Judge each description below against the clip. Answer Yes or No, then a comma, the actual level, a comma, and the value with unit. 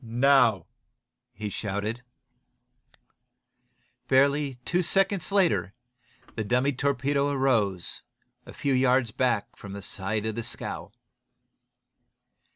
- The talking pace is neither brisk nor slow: No, slow, 105 wpm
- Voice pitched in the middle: No, low, 125 Hz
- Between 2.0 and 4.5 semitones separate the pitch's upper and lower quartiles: No, average, 5.0 semitones